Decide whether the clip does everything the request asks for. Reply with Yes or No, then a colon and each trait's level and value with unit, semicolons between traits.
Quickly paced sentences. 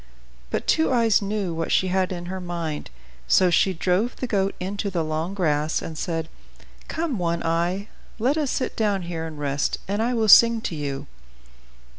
No: average, 185 wpm